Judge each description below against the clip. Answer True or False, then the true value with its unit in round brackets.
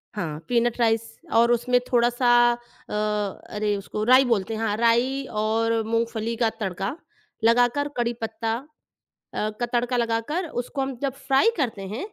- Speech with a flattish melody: True (1.9 semitones)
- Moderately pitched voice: False (230 Hz)